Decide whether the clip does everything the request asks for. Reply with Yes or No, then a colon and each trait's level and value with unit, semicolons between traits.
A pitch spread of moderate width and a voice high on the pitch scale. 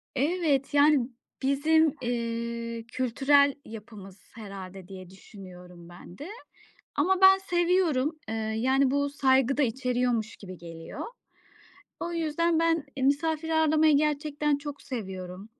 No: wide, 5.7 semitones; very high, 270 Hz